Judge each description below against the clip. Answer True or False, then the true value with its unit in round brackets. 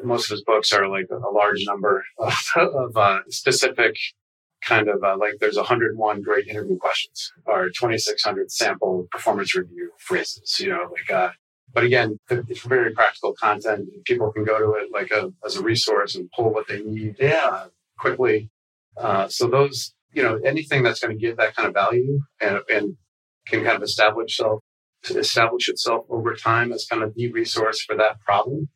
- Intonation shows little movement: False (4.4 semitones)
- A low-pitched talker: True (115 Hz)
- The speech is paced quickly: False (185 wpm)